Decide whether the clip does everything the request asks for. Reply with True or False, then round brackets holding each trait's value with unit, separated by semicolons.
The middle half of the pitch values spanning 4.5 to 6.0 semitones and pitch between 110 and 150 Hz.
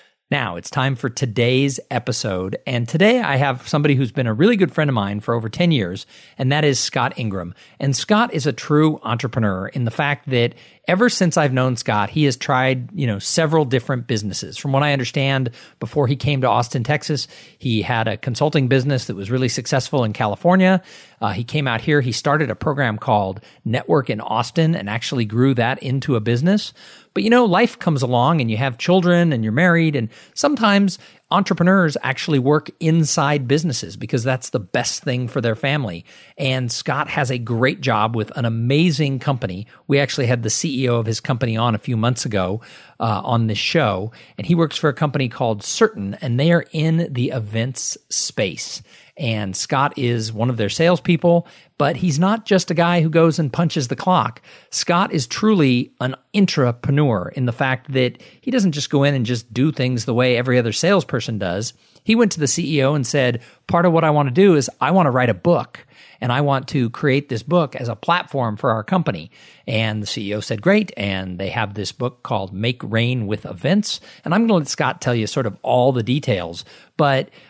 True (5.0 semitones; 135 Hz)